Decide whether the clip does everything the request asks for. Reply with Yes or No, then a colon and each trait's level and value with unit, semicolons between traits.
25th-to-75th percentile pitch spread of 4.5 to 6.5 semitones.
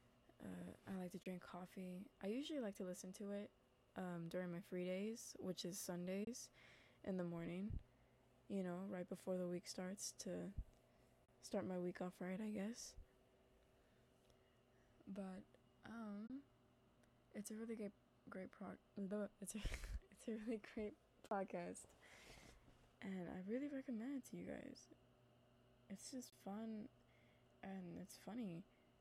No: average, 3.0 semitones